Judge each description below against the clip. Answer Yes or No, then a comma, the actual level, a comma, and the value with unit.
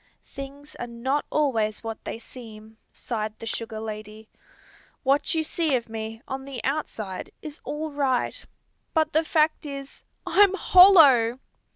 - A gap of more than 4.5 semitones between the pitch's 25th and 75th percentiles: Yes, average, 5.2 semitones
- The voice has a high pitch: Yes, very high, 265 Hz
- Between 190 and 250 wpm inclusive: No, average, 145 wpm